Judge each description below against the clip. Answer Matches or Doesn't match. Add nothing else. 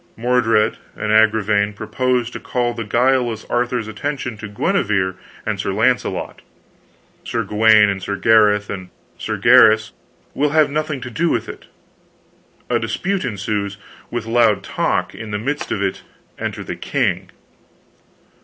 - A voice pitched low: Matches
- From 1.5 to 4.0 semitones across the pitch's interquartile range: Matches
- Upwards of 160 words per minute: Doesn't match